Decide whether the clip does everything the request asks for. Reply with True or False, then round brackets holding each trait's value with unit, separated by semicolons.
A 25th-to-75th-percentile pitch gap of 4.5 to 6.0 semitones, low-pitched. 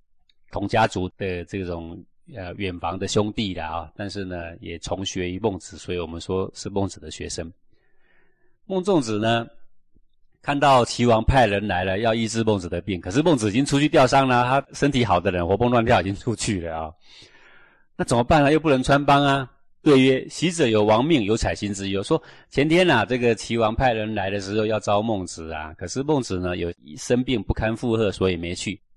True (5.4 semitones; 105 Hz)